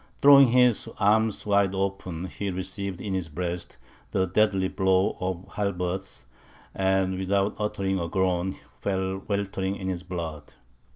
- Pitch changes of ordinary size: No, narrow, 1.5 semitones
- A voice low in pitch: Yes, very low, 95 Hz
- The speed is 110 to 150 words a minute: Yes, average, 140 wpm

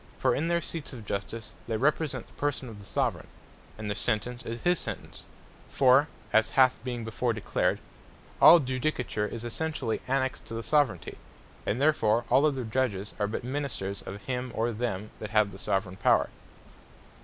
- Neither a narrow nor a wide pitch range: Yes, average, 3.9 semitones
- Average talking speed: Yes, average, 175 wpm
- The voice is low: Yes, low, 120 Hz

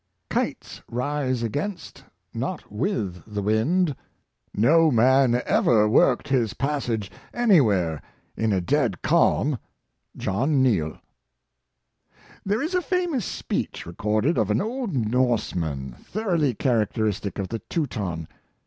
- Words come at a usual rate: No, slow, 115 wpm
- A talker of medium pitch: No, low, 120 Hz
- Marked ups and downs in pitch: Yes, wide, 6.2 semitones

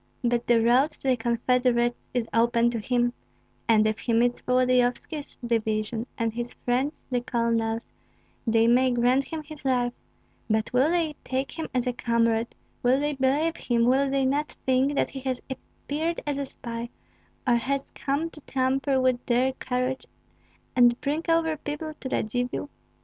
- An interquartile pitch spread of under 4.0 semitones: Yes, narrow, 2.5 semitones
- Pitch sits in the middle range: No, very high, 250 Hz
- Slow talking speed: No, average, 165 wpm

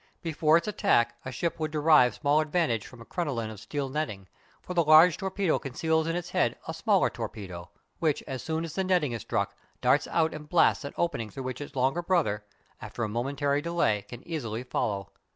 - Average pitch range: No, wide, 5.7 semitones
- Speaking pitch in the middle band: Yes, medium, 145 Hz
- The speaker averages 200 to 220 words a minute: Yes, fast, 205 wpm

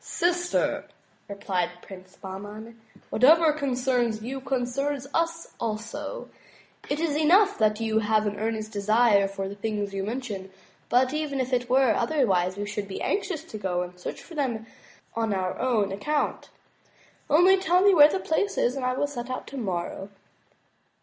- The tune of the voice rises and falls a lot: Yes, wide, 5.9 semitones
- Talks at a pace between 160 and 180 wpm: Yes, average, 165 wpm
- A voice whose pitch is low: No, high, 240 Hz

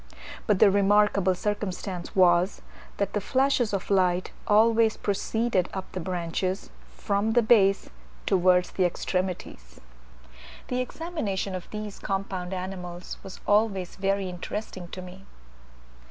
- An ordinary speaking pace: No, slow, 125 wpm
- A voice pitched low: No, high, 195 Hz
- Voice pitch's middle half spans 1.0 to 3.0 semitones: Yes, narrow, 2.4 semitones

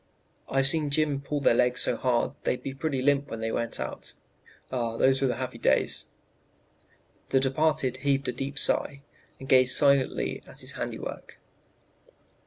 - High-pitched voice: No, low, 135 Hz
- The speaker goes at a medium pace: Yes, average, 160 wpm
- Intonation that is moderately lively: No, narrow, 1.9 semitones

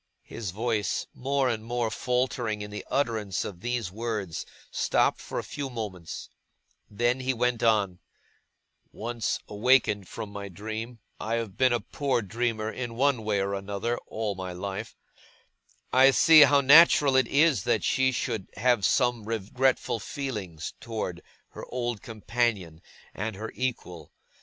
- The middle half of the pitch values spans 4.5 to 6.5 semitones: No, average, 3.5 semitones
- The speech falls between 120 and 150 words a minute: Yes, average, 145 wpm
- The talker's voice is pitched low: Yes, low, 115 Hz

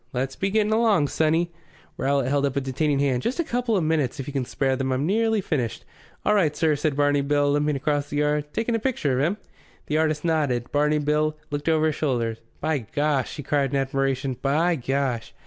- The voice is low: No, medium, 145 Hz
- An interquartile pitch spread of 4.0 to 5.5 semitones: No, average, 2.7 semitones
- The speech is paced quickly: Yes, fast, 215 wpm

